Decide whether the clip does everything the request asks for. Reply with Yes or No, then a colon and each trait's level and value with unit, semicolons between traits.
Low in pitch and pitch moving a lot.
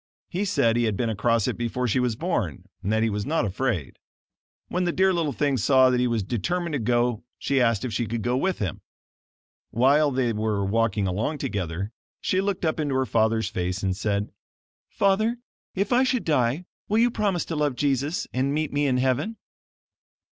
Yes: low, 125 Hz; wide, 6.0 semitones